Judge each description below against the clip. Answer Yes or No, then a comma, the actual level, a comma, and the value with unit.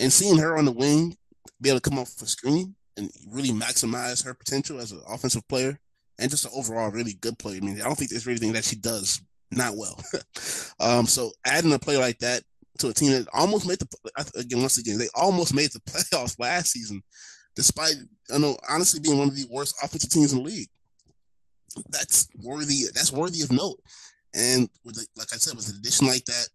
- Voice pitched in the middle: No, low, 125 Hz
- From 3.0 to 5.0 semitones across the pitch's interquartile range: Yes, average, 4.0 semitones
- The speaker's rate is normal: No, fast, 220 wpm